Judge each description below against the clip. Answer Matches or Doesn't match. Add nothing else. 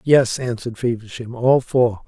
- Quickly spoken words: Doesn't match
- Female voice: Doesn't match